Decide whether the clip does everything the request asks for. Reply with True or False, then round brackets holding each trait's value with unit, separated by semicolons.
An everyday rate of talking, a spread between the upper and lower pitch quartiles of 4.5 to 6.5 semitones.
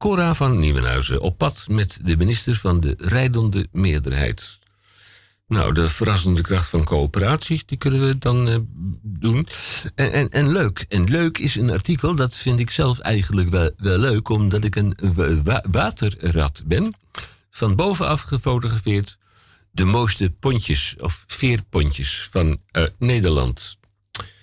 True (145 wpm; 5.1 semitones)